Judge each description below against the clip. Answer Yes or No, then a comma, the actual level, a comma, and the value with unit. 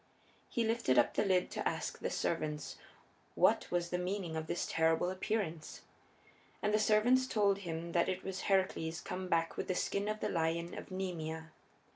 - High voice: No, medium, 180 Hz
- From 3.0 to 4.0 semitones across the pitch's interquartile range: Yes, average, 3.5 semitones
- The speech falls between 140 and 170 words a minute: No, average, 180 wpm